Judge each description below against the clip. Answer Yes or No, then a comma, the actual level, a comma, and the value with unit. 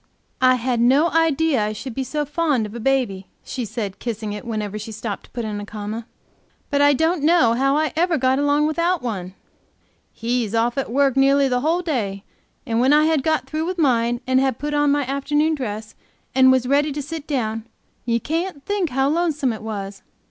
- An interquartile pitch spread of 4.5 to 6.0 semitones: Yes, average, 4.8 semitones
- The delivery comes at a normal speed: No, fast, 210 wpm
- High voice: Yes, very high, 265 Hz